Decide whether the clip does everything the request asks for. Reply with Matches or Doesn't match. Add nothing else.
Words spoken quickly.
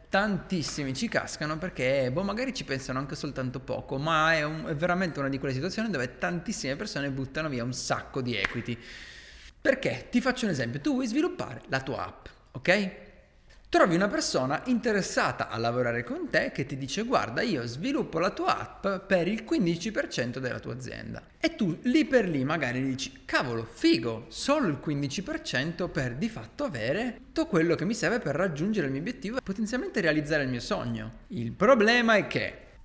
Matches